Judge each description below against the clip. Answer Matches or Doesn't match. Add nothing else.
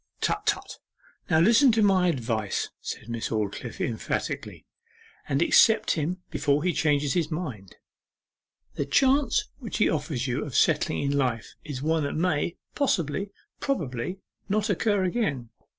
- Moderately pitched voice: Matches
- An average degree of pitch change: Doesn't match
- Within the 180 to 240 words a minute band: Doesn't match